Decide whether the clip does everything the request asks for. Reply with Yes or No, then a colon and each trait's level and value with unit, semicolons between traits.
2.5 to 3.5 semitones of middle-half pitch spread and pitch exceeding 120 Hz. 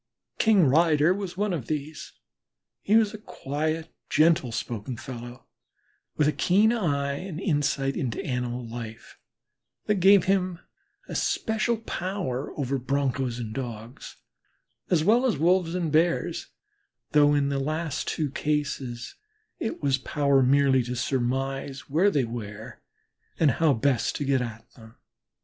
No: average, 5.1 semitones; medium, 140 Hz